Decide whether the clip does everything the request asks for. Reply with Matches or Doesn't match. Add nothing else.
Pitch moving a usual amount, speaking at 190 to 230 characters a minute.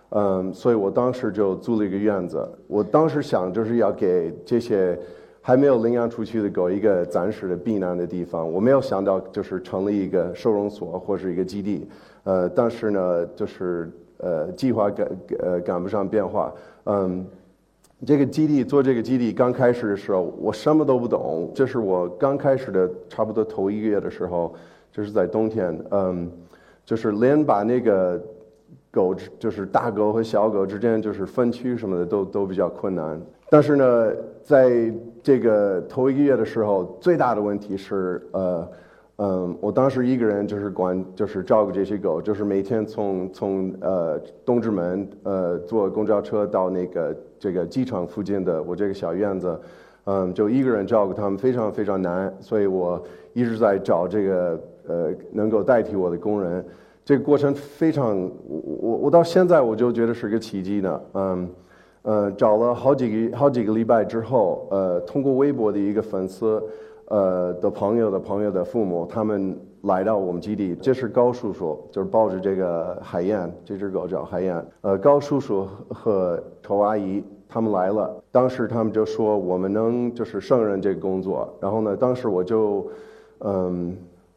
Doesn't match